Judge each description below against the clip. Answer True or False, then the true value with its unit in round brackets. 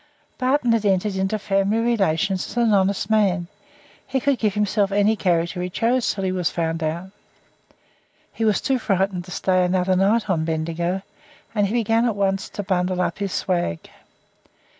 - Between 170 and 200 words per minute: True (175 wpm)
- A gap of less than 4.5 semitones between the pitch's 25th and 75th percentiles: True (3.1 semitones)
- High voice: True (195 Hz)